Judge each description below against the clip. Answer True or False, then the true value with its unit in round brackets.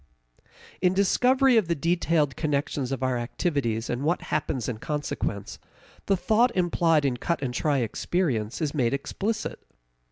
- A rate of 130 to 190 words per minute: True (150 wpm)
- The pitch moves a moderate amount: False (5.7 semitones)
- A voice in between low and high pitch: True (150 Hz)